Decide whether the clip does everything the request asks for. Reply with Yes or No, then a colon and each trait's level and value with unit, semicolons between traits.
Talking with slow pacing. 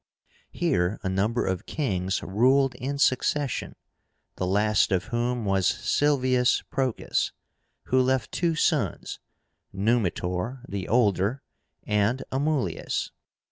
Yes: slow, 105 wpm